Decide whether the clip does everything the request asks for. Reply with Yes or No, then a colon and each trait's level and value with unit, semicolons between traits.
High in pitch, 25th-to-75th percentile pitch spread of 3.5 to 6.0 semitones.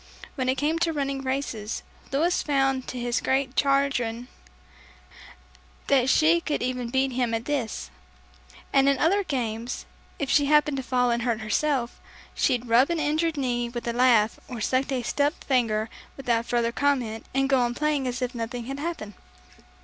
No: very high, 260 Hz; average, 2.9 semitones